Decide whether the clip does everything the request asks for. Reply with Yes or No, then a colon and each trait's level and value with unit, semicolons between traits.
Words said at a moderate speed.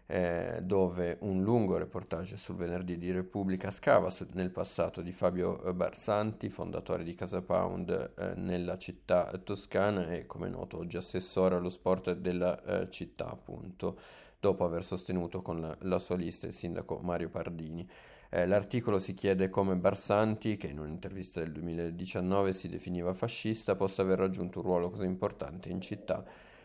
Yes: average, 155 wpm